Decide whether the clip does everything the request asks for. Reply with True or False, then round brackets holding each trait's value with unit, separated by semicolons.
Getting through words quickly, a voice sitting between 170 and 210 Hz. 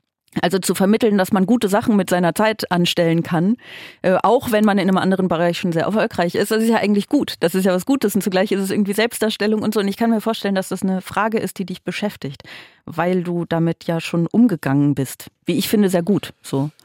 True (240 wpm; 190 Hz)